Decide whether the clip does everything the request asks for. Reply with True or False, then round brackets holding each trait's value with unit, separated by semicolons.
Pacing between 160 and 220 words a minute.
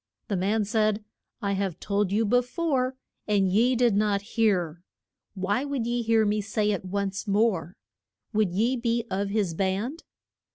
True (165 wpm)